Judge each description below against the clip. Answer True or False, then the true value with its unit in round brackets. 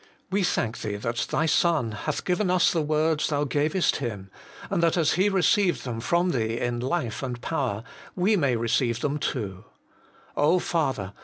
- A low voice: False (145 Hz)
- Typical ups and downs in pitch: False (6.6 semitones)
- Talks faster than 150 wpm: True (170 wpm)